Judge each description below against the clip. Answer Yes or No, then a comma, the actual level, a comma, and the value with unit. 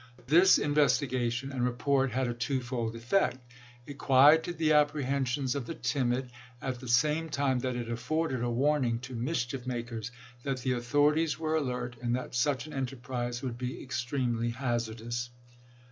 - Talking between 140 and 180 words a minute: Yes, average, 160 wpm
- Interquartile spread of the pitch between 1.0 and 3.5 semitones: Yes, average, 2.9 semitones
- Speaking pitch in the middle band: No, low, 130 Hz